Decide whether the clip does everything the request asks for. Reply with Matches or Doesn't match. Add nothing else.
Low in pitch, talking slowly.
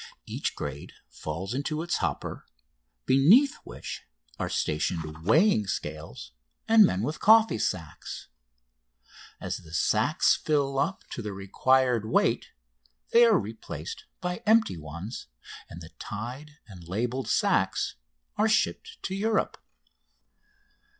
Matches